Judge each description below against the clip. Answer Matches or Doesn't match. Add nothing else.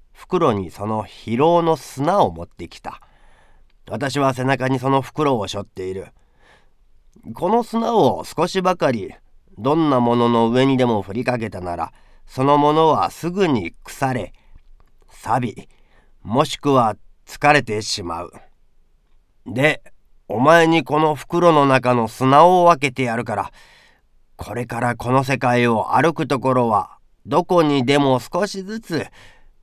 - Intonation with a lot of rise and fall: Matches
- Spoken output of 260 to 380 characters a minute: Doesn't match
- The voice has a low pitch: Matches